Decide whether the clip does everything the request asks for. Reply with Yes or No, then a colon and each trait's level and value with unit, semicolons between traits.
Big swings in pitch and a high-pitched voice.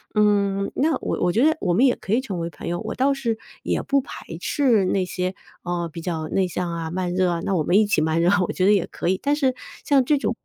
Yes: wide, 6.2 semitones; high, 195 Hz